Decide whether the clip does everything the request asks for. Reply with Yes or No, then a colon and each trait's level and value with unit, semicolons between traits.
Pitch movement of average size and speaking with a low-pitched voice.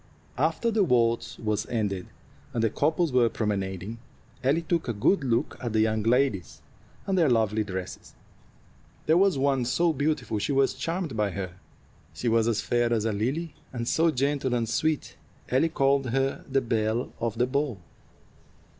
Yes: average, 4.6 semitones; low, 125 Hz